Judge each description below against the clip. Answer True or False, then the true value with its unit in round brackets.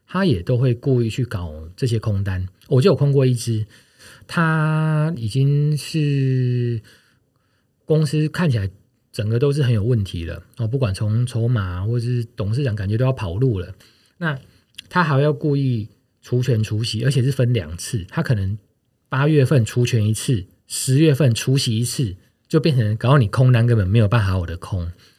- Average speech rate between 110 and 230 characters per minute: False (255 characters per minute)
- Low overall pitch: True (120 Hz)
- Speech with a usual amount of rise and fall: True (4.1 semitones)